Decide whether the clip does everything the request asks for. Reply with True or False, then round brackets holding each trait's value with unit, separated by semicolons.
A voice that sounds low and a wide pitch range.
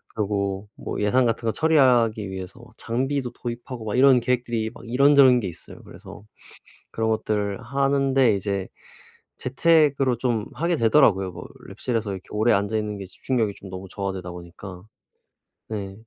False (110 Hz; 4.5 semitones)